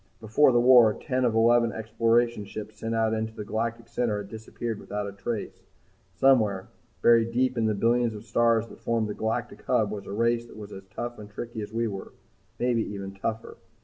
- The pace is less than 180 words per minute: No, average, 200 wpm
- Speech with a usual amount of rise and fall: No, narrow, 2.0 semitones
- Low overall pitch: Yes, low, 115 Hz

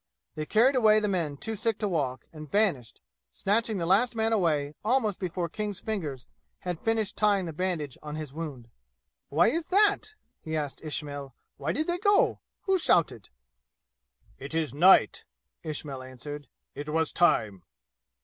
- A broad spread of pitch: Yes, wide, 6.7 semitones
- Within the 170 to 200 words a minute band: No, average, 160 wpm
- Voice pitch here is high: No, medium, 170 Hz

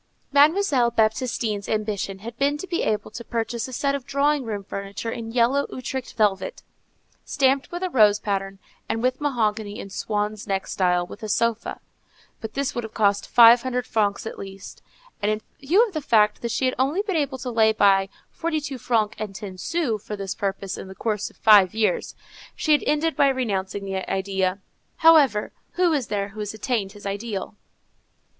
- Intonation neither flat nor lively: Yes, average, 4.6 semitones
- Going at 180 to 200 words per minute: Yes, average, 190 wpm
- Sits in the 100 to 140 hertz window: No, high, 220 Hz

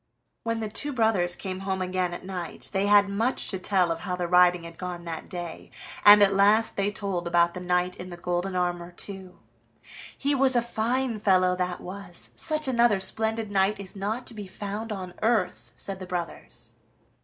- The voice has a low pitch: No, high, 190 Hz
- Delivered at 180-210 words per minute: Yes, average, 200 wpm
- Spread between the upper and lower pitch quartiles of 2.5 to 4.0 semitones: Yes, average, 3.0 semitones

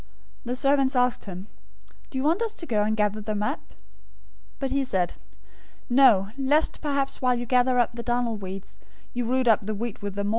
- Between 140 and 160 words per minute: No, average, 200 wpm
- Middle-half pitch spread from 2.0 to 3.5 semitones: No, average, 4.2 semitones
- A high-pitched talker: Yes, high, 240 Hz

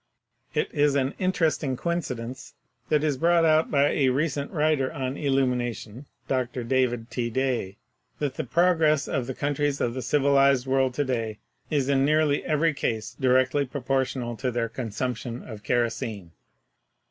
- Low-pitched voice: Yes, low, 130 Hz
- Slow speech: No, average, 155 wpm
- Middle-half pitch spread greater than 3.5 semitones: No, average, 3.0 semitones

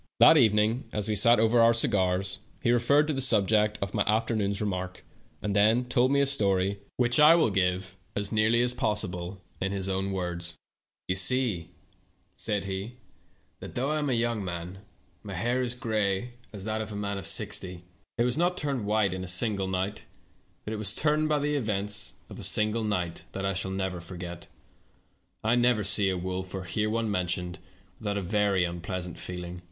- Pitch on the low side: Yes, low, 105 Hz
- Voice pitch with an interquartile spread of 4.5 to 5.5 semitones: No, average, 3.8 semitones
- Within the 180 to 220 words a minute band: Yes, average, 190 wpm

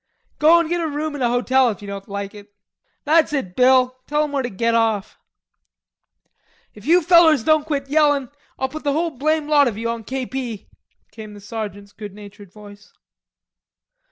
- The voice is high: Yes, very high, 255 Hz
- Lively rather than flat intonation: Yes, wide, 6.2 semitones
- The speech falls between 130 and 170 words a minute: No, average, 190 wpm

